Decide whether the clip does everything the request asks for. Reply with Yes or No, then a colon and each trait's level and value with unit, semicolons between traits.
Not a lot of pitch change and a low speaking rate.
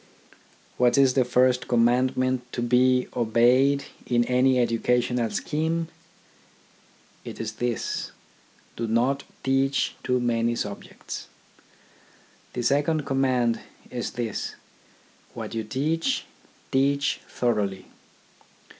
Yes: narrow, 2.2 semitones; slow, 100 wpm